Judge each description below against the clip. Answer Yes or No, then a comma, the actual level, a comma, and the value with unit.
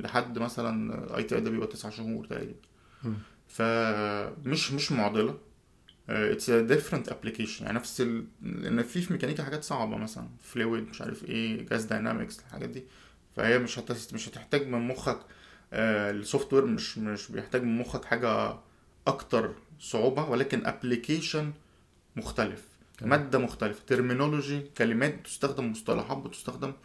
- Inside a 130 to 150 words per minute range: Yes, fast, 135 wpm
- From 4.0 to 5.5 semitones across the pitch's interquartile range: Yes, average, 4.3 semitones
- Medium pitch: No, low, 120 Hz